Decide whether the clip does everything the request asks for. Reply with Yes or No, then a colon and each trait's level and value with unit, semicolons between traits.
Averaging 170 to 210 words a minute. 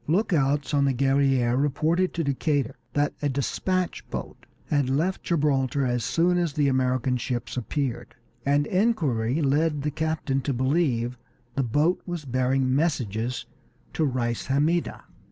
No: average, 140 wpm